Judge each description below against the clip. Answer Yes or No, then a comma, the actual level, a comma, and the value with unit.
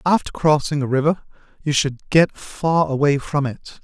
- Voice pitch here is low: No, medium, 150 Hz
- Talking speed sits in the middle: Yes, average, 170 wpm